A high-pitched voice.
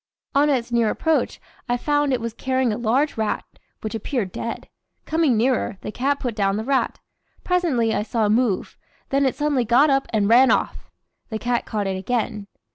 Yes: high, 240 Hz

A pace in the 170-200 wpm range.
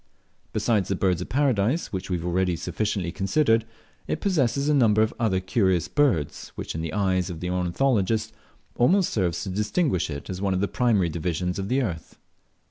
Yes: average, 190 wpm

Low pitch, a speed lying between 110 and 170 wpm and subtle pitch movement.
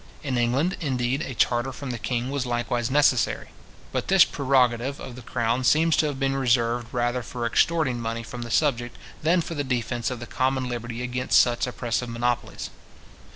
No: low, 125 Hz; average, 185 wpm; narrow, 2.3 semitones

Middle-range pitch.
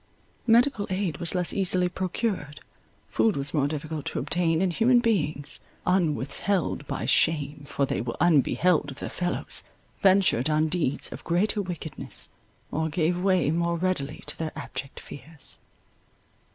Yes: medium, 170 Hz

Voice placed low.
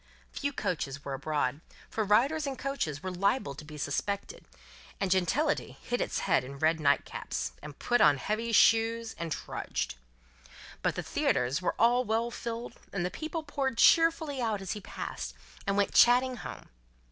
No: high, 215 Hz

